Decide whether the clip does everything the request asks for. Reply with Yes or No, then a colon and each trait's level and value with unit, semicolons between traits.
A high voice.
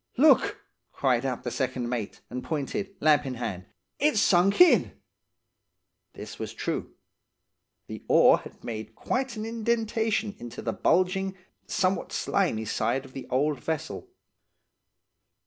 No: medium, 165 Hz